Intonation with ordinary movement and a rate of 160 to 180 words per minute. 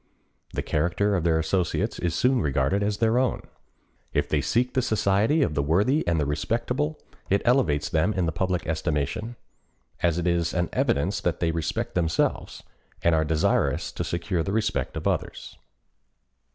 Yes: average, 4.8 semitones; average, 170 wpm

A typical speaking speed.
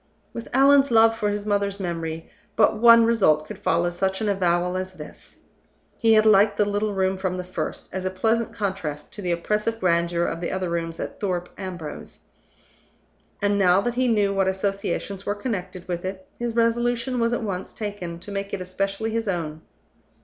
Yes: average, 190 wpm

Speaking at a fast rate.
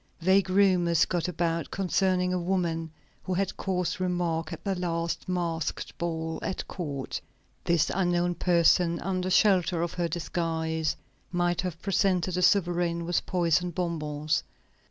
No: slow, 135 wpm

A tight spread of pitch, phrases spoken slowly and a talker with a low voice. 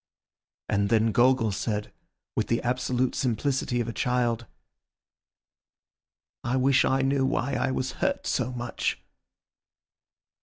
Yes: narrow, 2.1 semitones; slow, 120 wpm; low, 125 Hz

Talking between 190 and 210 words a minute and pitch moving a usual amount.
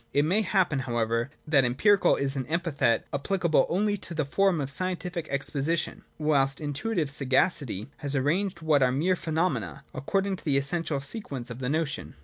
No: average, 175 wpm; average, 4.6 semitones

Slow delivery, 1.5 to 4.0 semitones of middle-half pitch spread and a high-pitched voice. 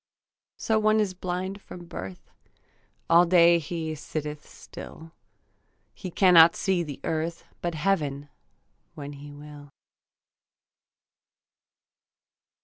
No: slow, 100 wpm; average, 3.4 semitones; medium, 165 Hz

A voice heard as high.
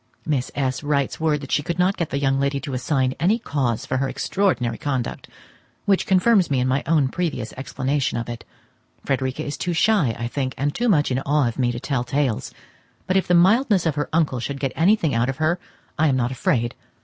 No: medium, 140 Hz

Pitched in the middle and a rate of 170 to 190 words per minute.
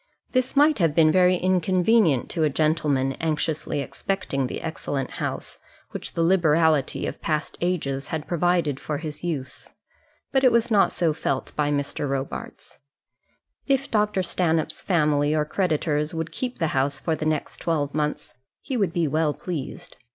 No: medium, 160 Hz; average, 160 wpm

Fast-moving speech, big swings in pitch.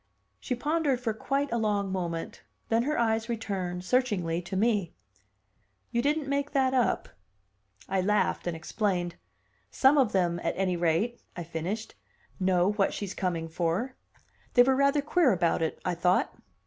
No: average, 160 wpm; wide, 6.2 semitones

